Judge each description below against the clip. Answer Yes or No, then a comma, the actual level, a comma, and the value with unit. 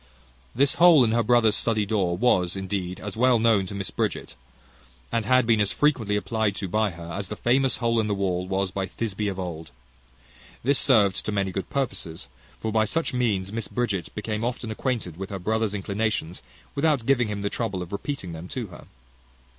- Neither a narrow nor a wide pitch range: Yes, average, 3.5 semitones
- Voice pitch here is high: No, low, 105 Hz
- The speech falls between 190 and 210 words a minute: Yes, average, 200 wpm